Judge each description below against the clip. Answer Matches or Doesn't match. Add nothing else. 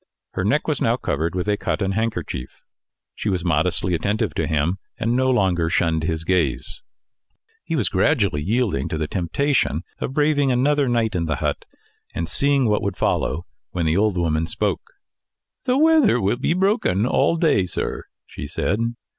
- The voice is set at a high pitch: Doesn't match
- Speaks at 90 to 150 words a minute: Doesn't match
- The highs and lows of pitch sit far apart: Matches